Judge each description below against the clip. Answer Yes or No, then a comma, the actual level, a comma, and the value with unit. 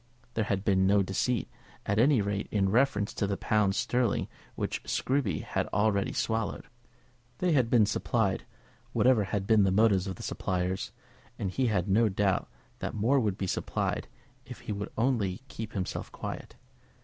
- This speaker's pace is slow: No, average, 170 wpm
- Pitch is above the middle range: No, low, 105 Hz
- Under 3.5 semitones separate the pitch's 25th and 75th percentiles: Yes, average, 3.0 semitones